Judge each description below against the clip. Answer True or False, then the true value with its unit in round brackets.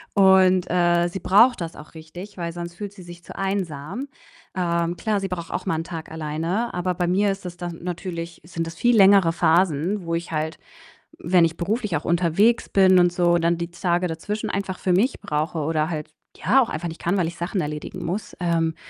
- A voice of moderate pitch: True (175 Hz)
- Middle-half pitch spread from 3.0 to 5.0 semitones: False (2.4 semitones)